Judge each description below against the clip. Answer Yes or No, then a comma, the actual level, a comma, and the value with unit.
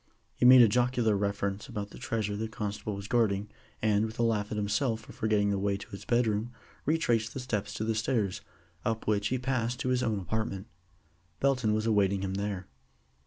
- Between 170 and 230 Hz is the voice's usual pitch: No, low, 110 Hz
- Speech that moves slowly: No, average, 200 wpm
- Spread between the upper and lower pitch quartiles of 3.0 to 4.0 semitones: No, narrow, 2.5 semitones